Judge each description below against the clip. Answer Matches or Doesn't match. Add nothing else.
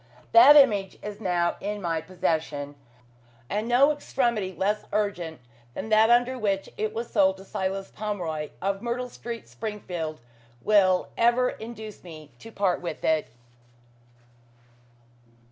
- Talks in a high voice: Matches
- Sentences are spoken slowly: Matches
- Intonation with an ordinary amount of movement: Matches